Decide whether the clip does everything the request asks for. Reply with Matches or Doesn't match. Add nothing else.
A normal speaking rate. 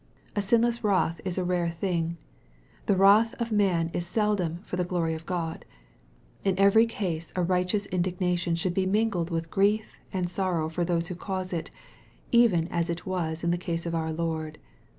Matches